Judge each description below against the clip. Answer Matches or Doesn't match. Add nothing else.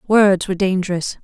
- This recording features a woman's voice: Matches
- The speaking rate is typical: Matches